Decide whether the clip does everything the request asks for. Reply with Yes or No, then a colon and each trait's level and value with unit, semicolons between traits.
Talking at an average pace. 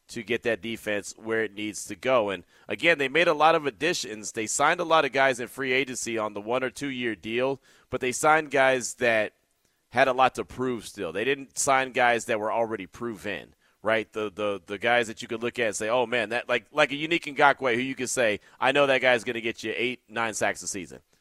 No: fast, 250 wpm